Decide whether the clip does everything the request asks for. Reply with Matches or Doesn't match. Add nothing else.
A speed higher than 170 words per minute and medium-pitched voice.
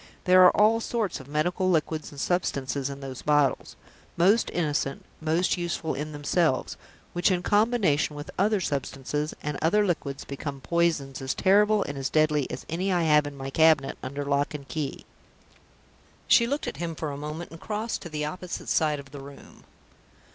Matches